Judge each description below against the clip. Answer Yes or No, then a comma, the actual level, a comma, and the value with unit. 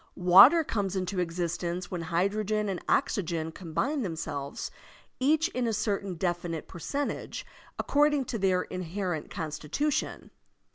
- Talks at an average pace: No, slow, 125 wpm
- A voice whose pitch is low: No, medium, 185 Hz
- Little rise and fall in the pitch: No, average, 5.2 semitones